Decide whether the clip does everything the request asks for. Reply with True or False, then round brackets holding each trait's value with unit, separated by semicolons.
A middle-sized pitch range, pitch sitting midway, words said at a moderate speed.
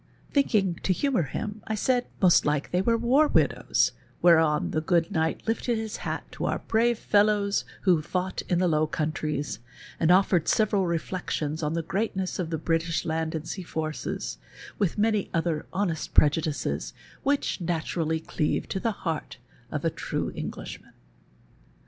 True (4.5 semitones; 175 Hz; 160 wpm)